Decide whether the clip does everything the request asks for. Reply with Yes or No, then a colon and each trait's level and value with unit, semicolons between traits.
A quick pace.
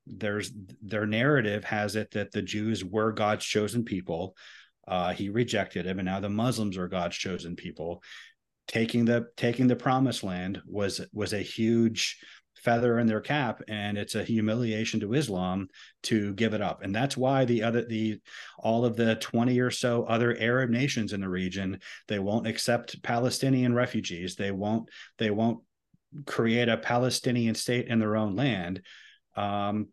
No: average, 170 wpm